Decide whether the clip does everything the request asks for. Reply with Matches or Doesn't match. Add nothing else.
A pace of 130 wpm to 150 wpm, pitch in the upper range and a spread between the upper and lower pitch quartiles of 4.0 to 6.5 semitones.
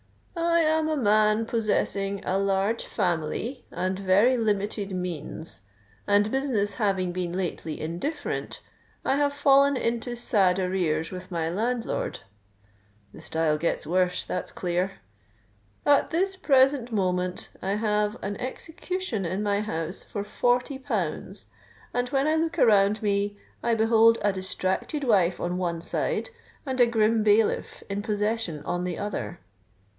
Matches